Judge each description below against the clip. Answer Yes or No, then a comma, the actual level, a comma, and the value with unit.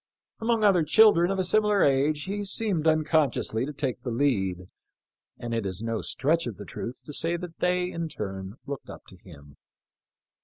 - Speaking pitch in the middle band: Yes, medium, 150 Hz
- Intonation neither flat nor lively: No, wide, 7.8 semitones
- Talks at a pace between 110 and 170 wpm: No, average, 185 wpm